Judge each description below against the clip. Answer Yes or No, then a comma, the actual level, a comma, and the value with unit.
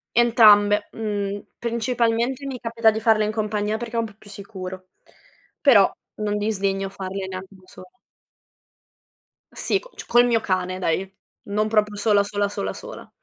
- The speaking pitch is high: Yes, high, 210 Hz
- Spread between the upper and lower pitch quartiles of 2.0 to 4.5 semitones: Yes, narrow, 2.5 semitones